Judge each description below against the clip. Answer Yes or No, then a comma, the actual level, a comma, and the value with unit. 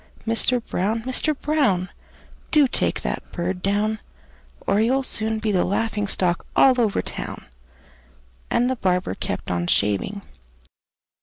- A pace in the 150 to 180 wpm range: No, slow, 135 wpm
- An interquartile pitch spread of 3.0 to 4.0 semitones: No, average, 4.9 semitones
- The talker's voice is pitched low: No, high, 215 Hz